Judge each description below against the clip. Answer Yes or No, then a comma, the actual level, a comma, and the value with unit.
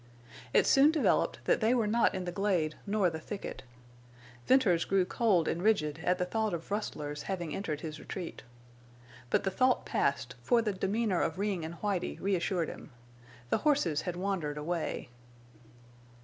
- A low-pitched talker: No, medium, 185 Hz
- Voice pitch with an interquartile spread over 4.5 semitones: No, average, 4.1 semitones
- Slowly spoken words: No, average, 165 wpm